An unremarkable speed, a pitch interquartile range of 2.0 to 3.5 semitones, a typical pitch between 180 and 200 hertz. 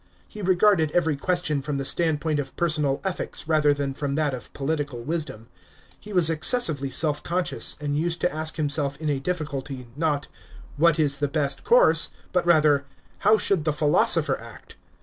No: average, 180 wpm; average, 2.9 semitones; medium, 150 Hz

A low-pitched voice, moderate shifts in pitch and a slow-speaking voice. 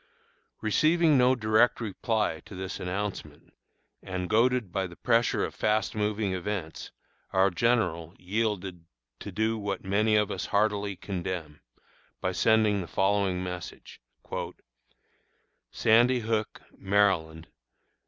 Yes: low, 100 Hz; average, 3.1 semitones; slow, 115 wpm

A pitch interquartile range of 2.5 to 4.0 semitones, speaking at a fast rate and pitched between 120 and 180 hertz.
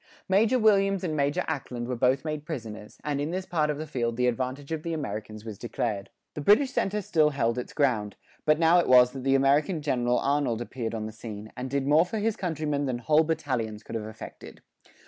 No: average, 5.0 semitones; fast, 220 wpm; medium, 140 Hz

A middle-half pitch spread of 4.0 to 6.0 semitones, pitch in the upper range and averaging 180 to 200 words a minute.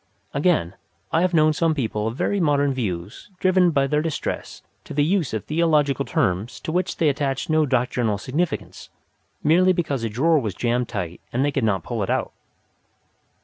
No: wide, 5.5 semitones; medium, 140 Hz; average, 185 wpm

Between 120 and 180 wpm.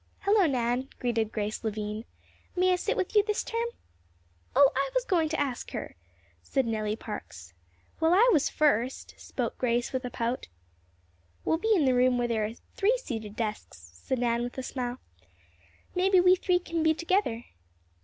Yes: average, 175 wpm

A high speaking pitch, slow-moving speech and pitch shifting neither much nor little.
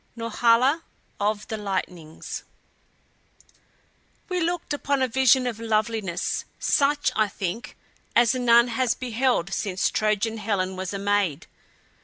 Yes: high, 225 Hz; slow, 120 wpm; average, 3.9 semitones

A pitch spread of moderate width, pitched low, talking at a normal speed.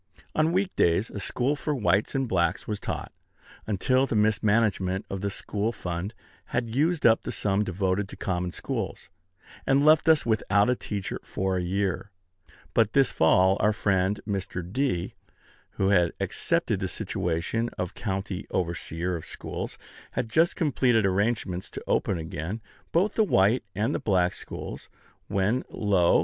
Yes: average, 4.3 semitones; low, 100 Hz; average, 160 wpm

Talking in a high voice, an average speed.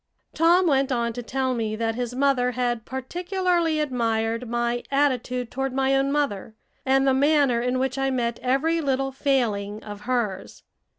Yes: very high, 255 Hz; average, 165 wpm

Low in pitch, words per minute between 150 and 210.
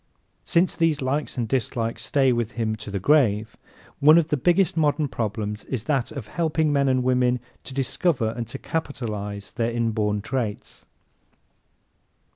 Yes: low, 125 Hz; average, 155 wpm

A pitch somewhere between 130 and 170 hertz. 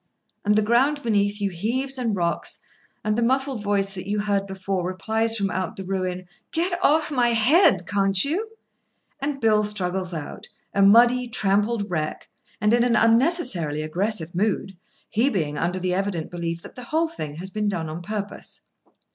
No: high, 205 Hz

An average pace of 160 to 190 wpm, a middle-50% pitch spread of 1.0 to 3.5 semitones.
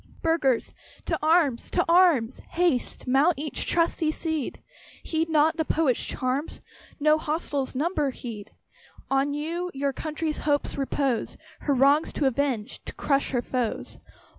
No: average, 140 wpm; average, 3.1 semitones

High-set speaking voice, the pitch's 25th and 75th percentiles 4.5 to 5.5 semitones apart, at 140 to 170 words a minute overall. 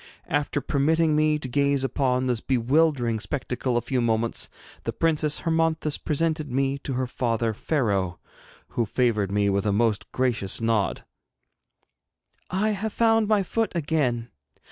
No: low, 135 Hz; average, 5.1 semitones; average, 145 wpm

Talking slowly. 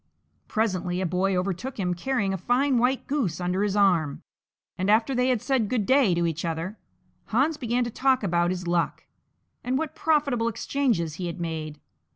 No: average, 185 wpm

